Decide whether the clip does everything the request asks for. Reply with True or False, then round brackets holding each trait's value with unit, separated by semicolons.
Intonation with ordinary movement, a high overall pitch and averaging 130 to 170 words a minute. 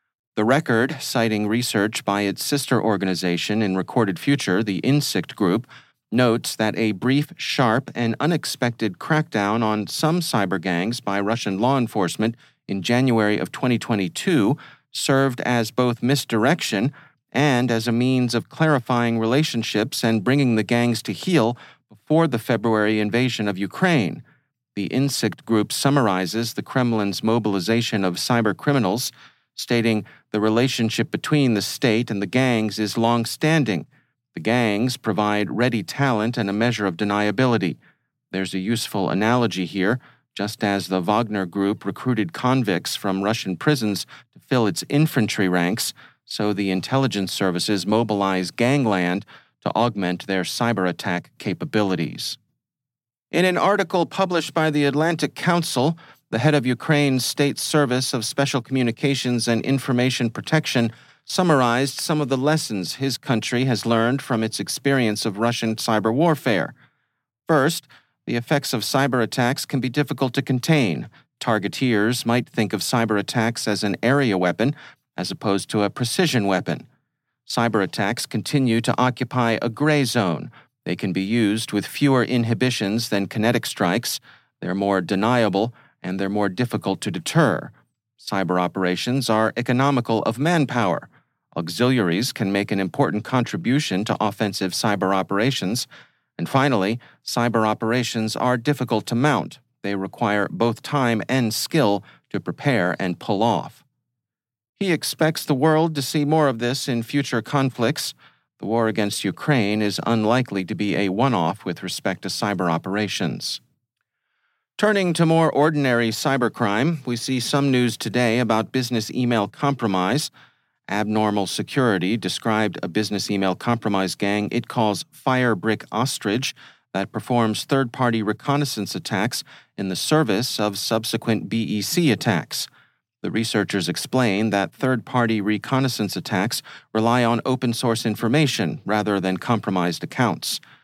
False (4.1 semitones; 115 Hz; 140 wpm)